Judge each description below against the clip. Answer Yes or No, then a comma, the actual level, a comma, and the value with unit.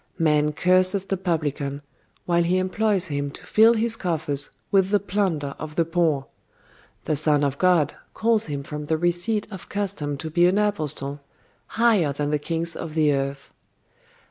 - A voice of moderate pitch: Yes, medium, 165 Hz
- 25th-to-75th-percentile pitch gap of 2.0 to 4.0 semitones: No, average, 4.5 semitones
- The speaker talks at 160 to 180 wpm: Yes, average, 170 wpm